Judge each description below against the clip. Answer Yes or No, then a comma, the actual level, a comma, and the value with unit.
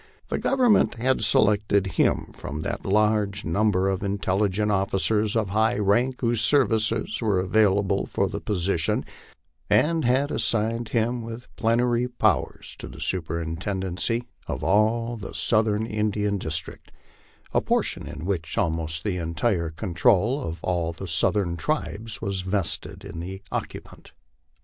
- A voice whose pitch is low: Yes, low, 105 Hz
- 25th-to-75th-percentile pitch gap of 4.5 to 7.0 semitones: No, average, 3.6 semitones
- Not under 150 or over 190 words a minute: No, average, 140 wpm